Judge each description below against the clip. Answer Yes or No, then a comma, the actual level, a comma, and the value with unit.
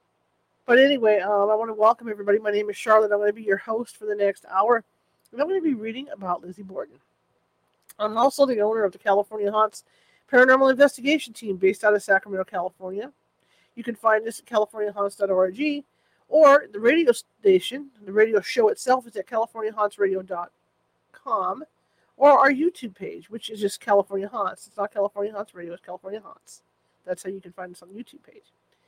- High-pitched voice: Yes, high, 215 Hz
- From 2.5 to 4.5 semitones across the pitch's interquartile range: Yes, average, 4.2 semitones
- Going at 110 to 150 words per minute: No, average, 190 wpm